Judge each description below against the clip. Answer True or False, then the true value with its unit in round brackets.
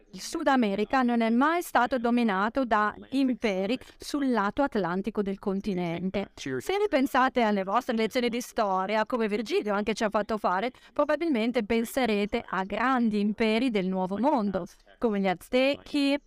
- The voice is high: True (230 Hz)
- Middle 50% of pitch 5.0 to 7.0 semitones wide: False (4.2 semitones)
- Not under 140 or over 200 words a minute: True (150 wpm)